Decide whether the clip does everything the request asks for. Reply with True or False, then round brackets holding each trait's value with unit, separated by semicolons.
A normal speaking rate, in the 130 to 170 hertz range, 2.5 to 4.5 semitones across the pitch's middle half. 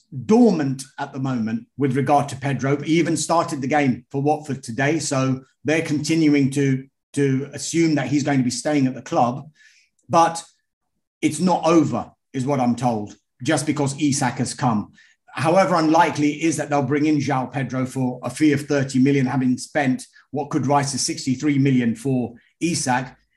True (175 wpm; 140 Hz; 2.8 semitones)